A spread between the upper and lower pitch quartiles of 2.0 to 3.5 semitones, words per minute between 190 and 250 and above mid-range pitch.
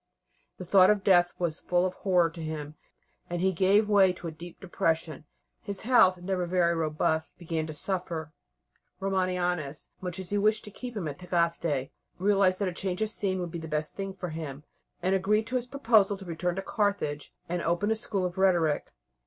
No: average, 2.9 semitones; average, 200 wpm; medium, 180 Hz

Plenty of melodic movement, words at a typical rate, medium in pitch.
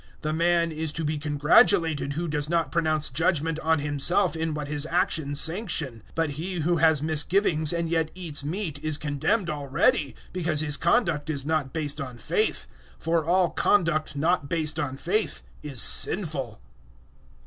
No: narrow, 2.5 semitones; average, 165 wpm; medium, 155 Hz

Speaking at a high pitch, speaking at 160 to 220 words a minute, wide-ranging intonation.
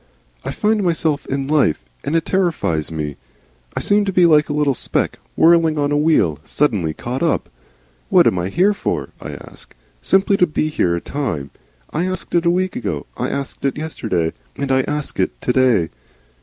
No: medium, 145 Hz; average, 195 wpm; wide, 8.0 semitones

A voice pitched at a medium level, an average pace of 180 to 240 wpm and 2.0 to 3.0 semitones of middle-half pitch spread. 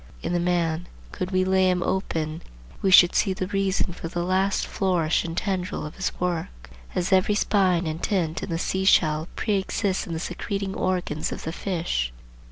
Yes: medium, 180 Hz; average, 185 wpm; narrow, 2.5 semitones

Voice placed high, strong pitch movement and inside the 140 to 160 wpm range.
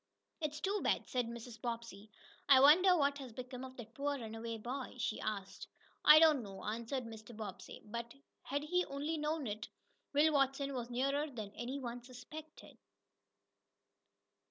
No: very high, 255 Hz; average, 3.8 semitones; average, 155 wpm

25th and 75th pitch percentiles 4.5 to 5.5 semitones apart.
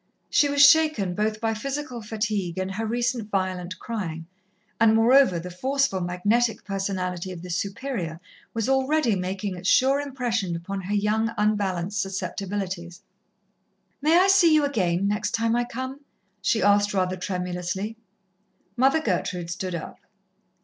Yes: average, 4.8 semitones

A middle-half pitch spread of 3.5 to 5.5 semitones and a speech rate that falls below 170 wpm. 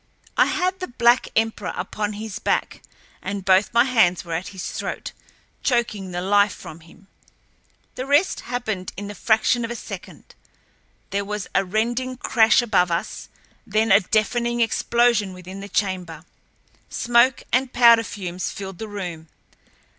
Yes: average, 4.0 semitones; average, 155 wpm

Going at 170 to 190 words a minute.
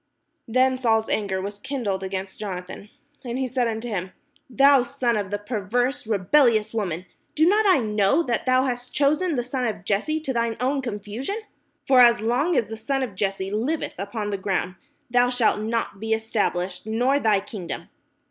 Yes: average, 185 wpm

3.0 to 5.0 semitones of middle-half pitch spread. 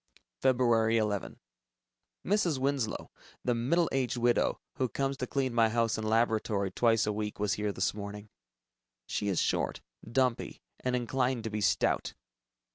Yes: average, 3.4 semitones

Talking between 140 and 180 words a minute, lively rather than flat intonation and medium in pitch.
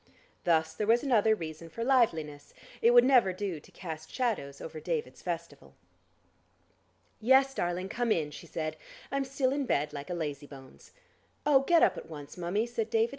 Yes: average, 175 wpm; wide, 7.3 semitones; medium, 180 Hz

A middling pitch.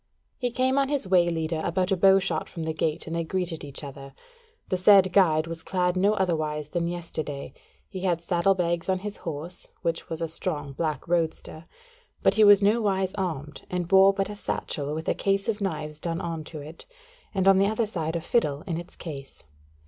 Yes: medium, 175 Hz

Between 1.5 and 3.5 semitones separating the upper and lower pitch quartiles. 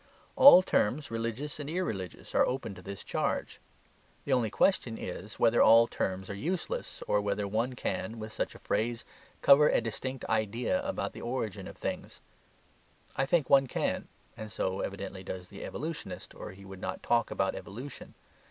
No: average, 5.0 semitones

